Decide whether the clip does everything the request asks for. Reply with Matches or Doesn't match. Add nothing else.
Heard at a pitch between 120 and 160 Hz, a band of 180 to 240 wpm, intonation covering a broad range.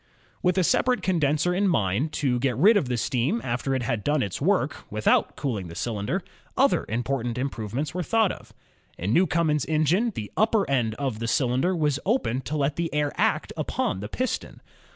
Matches